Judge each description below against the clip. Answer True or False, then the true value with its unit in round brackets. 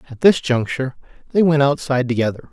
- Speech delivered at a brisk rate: False (165 wpm)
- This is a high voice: False (135 Hz)